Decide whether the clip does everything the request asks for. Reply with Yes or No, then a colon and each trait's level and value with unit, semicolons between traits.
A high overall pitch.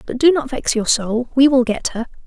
Yes: very high, 250 Hz